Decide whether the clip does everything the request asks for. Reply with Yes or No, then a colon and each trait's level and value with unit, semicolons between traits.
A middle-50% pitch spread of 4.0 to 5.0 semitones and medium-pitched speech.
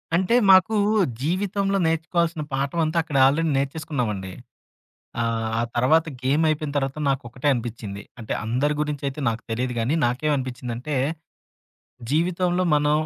Yes: average, 4.7 semitones; medium, 145 Hz